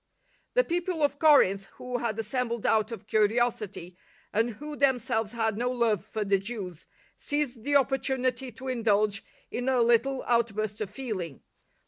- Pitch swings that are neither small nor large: Yes, average, 3.7 semitones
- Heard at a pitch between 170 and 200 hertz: No, high, 235 Hz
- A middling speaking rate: Yes, average, 150 wpm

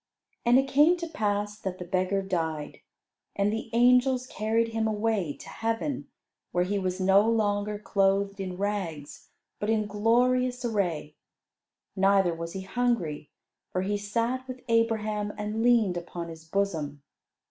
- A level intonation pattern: No, average, 3.5 semitones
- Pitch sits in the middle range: No, high, 205 Hz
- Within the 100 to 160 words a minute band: Yes, average, 145 wpm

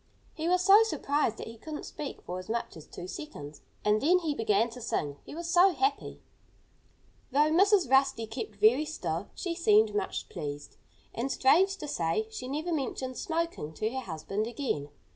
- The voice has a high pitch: Yes, very high, 255 Hz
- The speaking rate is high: No, average, 180 wpm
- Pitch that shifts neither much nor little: No, wide, 7.4 semitones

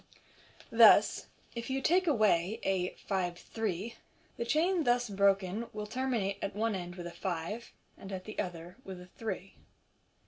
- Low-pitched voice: No, high, 200 Hz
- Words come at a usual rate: Yes, average, 165 wpm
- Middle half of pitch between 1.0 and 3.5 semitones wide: No, average, 4.3 semitones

